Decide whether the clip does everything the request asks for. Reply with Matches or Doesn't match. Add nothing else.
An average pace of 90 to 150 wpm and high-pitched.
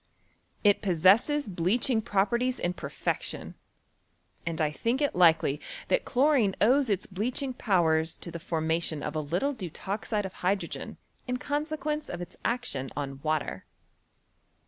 Matches